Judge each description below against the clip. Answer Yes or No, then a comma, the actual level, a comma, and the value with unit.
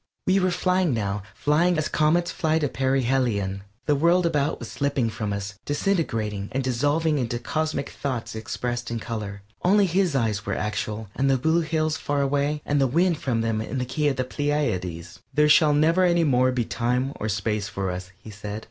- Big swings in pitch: Yes, wide, 5.9 semitones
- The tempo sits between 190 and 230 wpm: Yes, average, 195 wpm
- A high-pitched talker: No, low, 135 Hz